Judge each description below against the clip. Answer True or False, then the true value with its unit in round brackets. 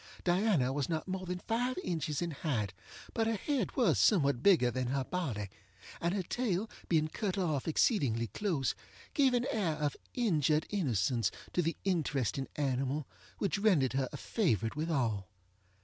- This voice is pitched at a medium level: True (160 Hz)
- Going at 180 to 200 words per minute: False (165 wpm)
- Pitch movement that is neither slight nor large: False (6.6 semitones)